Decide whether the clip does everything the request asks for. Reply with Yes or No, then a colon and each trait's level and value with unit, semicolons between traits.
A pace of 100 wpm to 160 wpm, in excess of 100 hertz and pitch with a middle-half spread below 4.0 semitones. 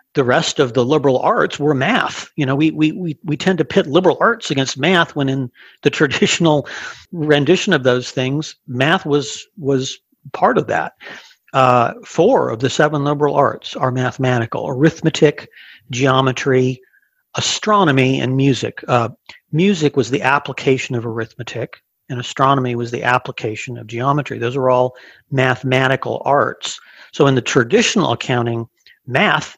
Yes: average, 150 wpm; low, 135 Hz; average, 3.4 semitones